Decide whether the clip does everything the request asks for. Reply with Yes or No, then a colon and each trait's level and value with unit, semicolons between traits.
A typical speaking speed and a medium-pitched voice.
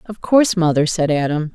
Yes: average, 195 wpm; medium, 170 Hz